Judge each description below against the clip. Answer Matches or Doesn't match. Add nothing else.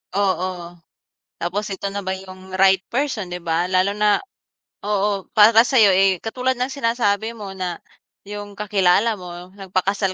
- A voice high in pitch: Matches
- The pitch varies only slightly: Matches